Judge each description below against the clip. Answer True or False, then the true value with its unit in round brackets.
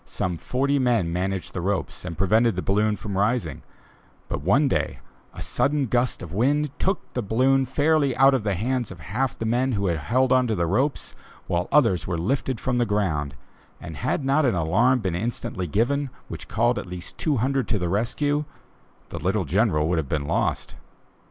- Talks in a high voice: False (110 Hz)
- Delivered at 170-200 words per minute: True (195 wpm)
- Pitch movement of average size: False (6.3 semitones)